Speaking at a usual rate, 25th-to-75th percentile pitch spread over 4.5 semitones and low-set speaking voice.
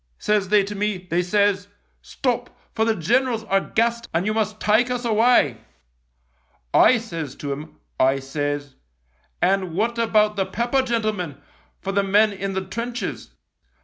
No: average, 170 wpm; average, 4.9 semitones; high, 205 Hz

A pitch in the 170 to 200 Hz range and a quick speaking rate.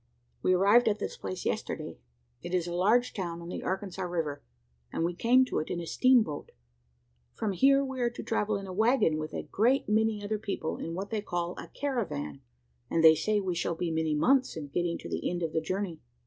Yes: medium, 185 Hz; fast, 225 wpm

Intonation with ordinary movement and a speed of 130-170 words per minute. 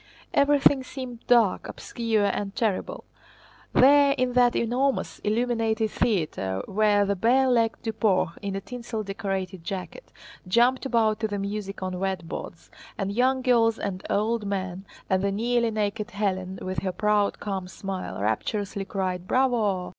Yes: average, 3.6 semitones; average, 145 wpm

